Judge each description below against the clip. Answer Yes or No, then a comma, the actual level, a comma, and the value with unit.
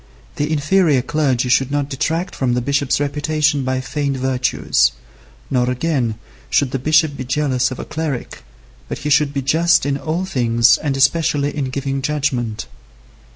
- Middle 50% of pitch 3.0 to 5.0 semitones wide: No, narrow, 2.6 semitones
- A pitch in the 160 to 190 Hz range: No, medium, 140 Hz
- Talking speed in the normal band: Yes, average, 160 wpm